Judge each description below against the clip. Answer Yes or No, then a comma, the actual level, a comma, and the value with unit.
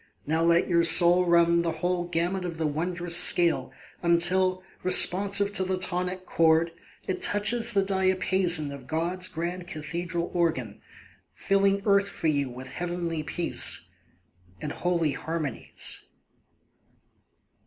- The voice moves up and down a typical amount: No, narrow, 2.1 semitones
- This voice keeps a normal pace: No, slow, 125 wpm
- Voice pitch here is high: No, medium, 175 Hz